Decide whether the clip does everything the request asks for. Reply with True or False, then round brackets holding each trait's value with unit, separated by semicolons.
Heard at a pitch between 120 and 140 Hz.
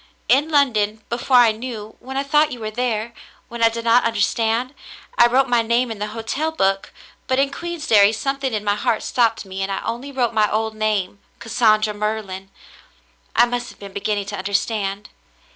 False (225 Hz)